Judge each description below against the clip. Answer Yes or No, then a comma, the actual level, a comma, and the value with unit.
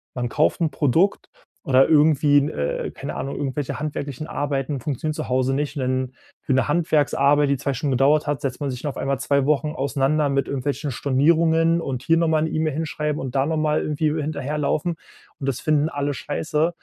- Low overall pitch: No, medium, 145 Hz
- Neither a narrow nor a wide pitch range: No, narrow, 2.2 semitones